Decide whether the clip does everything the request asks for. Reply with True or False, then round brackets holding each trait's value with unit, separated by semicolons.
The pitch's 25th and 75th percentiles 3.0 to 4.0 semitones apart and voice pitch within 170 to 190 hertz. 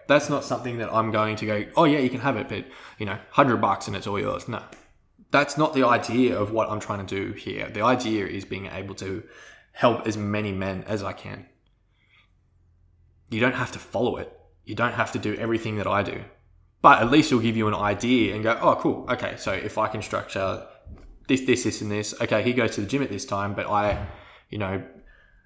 False (3.7 semitones; 110 Hz)